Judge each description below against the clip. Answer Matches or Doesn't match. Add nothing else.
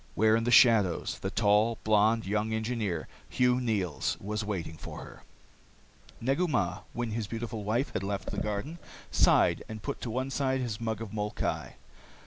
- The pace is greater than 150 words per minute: Matches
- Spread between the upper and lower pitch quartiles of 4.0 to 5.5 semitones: Doesn't match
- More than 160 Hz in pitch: Doesn't match